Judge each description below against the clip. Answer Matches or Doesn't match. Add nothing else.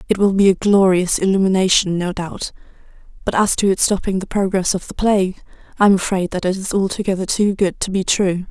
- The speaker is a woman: Matches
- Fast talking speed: Matches